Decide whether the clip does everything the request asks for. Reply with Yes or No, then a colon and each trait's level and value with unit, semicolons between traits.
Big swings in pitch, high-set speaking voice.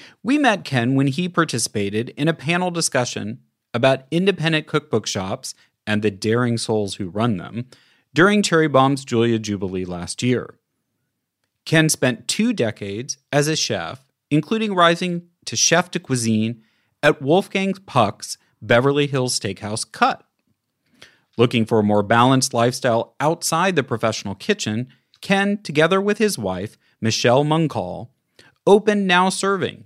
No: wide, 6.8 semitones; low, 130 Hz